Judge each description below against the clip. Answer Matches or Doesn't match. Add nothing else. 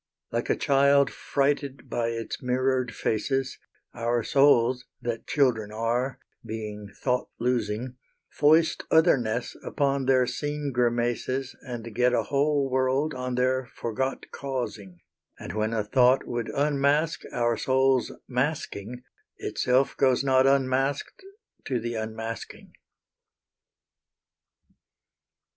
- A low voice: Matches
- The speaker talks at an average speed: Doesn't match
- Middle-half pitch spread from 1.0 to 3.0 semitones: Matches